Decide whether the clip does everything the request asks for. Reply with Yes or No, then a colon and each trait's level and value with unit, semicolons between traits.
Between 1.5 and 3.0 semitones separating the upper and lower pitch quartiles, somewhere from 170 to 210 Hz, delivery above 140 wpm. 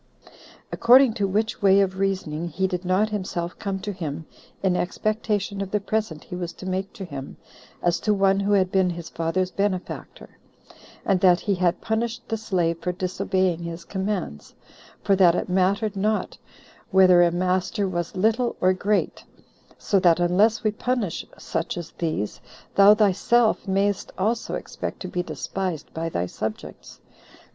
Yes: average, 2.7 semitones; high, 190 Hz; average, 165 wpm